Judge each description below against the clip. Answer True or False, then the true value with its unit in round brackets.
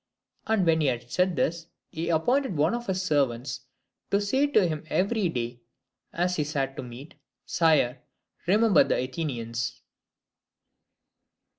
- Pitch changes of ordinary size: False (6.5 semitones)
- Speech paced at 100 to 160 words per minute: True (140 wpm)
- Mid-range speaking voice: True (160 Hz)